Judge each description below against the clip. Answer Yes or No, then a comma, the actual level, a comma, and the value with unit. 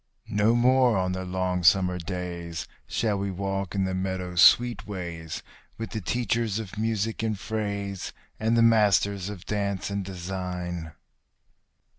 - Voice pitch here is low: Yes, low, 100 Hz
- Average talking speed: Yes, average, 145 wpm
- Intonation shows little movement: No, average, 3.2 semitones